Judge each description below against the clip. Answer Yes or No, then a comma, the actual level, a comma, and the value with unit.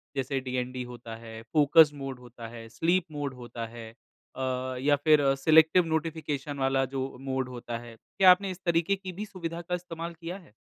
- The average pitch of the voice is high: No, medium, 145 Hz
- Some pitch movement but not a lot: Yes, average, 5.0 semitones